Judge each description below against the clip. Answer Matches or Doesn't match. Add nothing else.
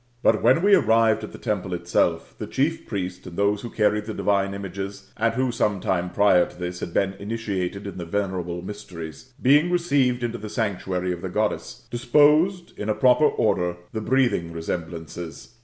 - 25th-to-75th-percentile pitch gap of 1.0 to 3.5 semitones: Doesn't match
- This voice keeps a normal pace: Matches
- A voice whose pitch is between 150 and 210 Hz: Doesn't match